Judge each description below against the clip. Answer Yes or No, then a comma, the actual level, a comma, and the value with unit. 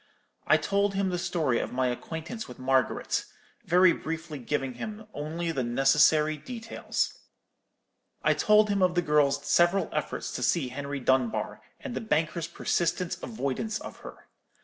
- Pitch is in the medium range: Yes, medium, 160 Hz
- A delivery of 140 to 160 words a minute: Yes, average, 150 wpm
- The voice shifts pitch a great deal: Yes, wide, 5.7 semitones